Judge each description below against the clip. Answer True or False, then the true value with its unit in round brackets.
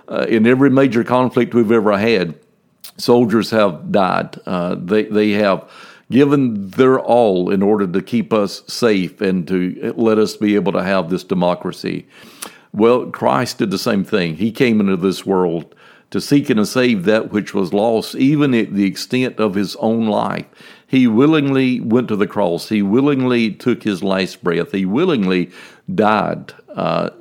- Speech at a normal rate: True (170 wpm)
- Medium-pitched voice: False (110 Hz)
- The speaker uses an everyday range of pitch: True (4.1 semitones)